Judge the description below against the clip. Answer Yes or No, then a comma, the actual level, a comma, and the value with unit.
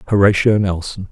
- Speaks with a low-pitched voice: Yes, low, 100 Hz